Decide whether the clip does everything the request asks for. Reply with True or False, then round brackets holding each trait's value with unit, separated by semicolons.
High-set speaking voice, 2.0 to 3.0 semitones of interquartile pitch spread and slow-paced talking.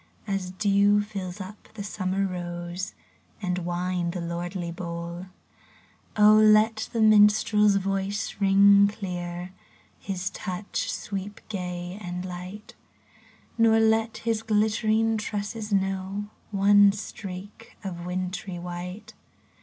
True (195 Hz; 2.7 semitones; 105 wpm)